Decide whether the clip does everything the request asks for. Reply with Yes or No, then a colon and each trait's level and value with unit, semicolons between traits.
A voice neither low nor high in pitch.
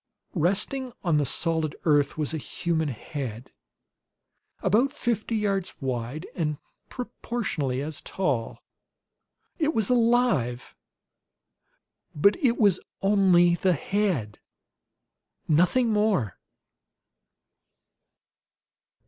Yes: medium, 175 Hz